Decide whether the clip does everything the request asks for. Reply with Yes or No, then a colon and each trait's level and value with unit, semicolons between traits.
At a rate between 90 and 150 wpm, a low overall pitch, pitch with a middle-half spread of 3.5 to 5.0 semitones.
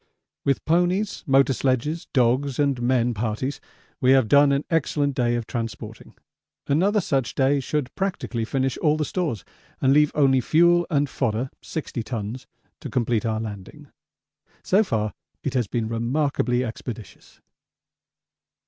Yes: average, 140 wpm; low, 130 Hz; average, 3.8 semitones